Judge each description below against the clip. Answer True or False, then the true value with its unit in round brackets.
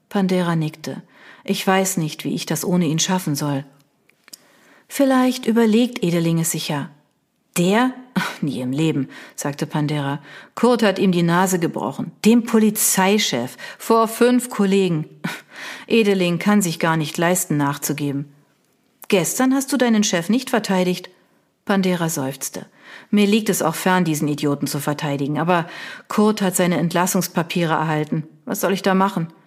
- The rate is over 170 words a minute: False (145 wpm)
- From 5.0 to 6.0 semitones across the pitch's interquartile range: True (5.6 semitones)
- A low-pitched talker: False (180 Hz)